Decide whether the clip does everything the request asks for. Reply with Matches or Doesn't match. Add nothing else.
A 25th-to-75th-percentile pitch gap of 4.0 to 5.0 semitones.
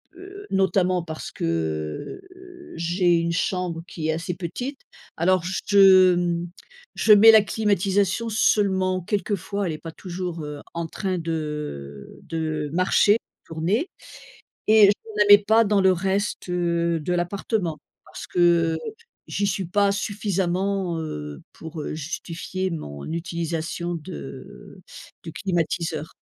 Doesn't match